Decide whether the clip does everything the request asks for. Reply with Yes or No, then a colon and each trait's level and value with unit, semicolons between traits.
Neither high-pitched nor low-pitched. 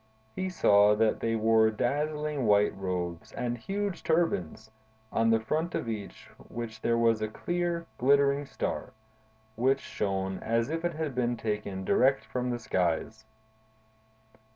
No: low, 115 Hz